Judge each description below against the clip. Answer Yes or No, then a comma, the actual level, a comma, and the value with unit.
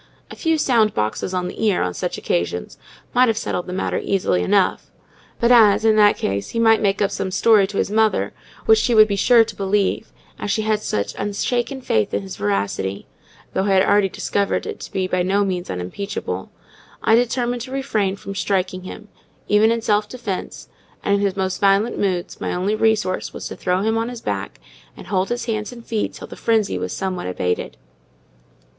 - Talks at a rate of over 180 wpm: Yes, average, 200 wpm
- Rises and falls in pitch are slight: No, average, 3.2 semitones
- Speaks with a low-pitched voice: No, high, 205 Hz